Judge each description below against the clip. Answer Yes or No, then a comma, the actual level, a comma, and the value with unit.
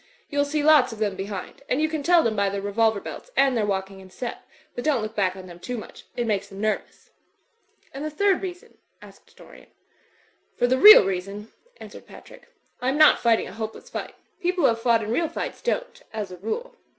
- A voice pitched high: Yes, high, 230 Hz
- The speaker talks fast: Yes, fast, 220 wpm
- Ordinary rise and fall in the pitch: No, wide, 7.0 semitones